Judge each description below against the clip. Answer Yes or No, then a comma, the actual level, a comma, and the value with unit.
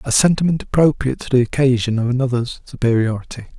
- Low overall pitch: Yes, low, 130 Hz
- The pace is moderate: Yes, average, 150 wpm